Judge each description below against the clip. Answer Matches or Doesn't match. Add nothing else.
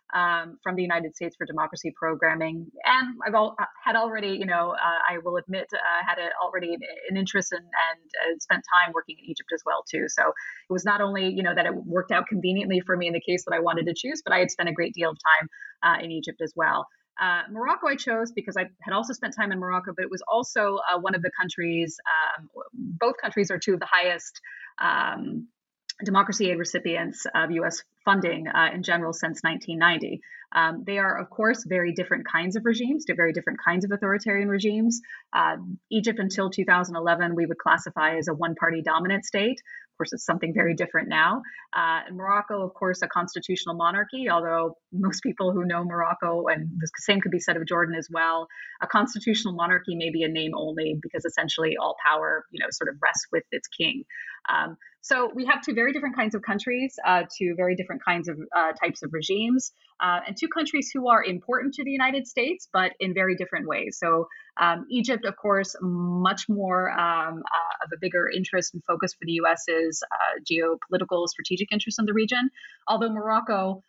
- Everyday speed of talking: Doesn't match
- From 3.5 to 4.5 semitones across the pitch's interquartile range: Matches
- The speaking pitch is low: Doesn't match